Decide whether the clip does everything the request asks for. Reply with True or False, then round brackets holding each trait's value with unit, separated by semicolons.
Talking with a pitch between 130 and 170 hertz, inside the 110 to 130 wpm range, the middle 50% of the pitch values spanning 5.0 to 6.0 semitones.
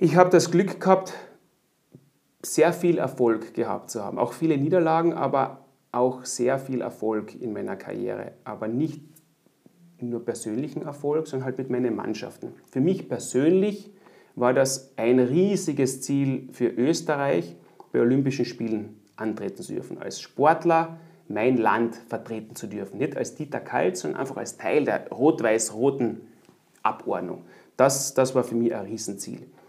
False (135 Hz; 150 wpm; 5.5 semitones)